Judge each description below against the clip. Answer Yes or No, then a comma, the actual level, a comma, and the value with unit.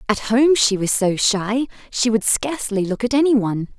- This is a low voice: No, high, 230 Hz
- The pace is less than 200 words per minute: No, fast, 205 wpm